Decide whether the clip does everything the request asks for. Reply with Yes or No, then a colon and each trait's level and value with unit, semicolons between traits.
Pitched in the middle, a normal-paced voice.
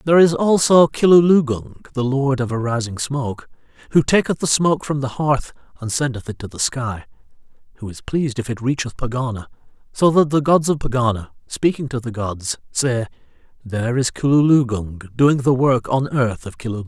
No: low, 130 Hz; average, 180 wpm